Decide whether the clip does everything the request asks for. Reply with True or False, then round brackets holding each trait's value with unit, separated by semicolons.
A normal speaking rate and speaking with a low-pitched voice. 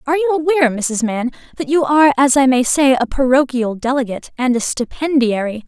False (190 wpm; 265 Hz)